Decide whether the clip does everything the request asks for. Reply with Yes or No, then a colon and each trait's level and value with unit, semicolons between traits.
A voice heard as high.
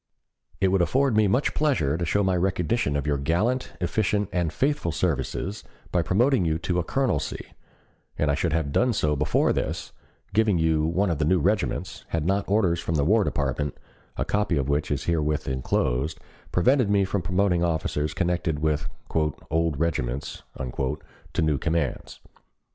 No: very low, 85 Hz